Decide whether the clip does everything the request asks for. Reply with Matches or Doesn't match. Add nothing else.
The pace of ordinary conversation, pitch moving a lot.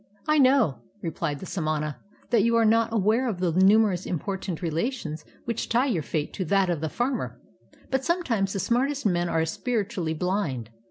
Matches